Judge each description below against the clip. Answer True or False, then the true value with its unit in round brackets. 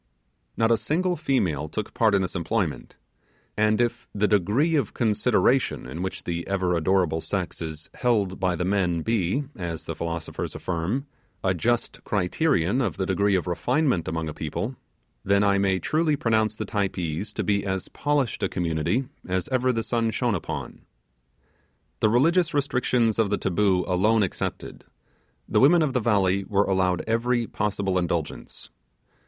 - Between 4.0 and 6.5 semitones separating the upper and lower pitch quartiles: True (5.0 semitones)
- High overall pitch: False (100 Hz)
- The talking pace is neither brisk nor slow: True (160 wpm)